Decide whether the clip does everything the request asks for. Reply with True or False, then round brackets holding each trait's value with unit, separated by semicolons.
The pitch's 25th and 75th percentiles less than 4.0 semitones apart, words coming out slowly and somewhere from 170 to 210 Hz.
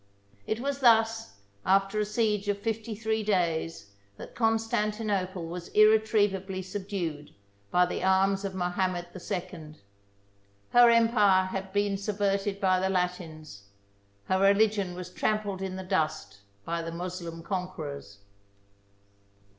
True (3.0 semitones; 125 wpm; 190 Hz)